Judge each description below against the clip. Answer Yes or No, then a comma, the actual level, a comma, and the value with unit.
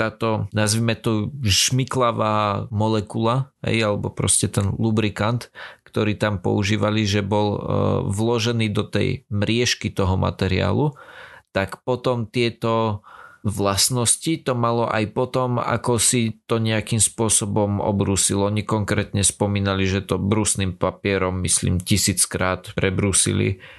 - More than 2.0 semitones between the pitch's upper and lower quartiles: Yes, narrow, 2.6 semitones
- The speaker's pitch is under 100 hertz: No, low, 105 Hz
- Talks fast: No, average, 115 wpm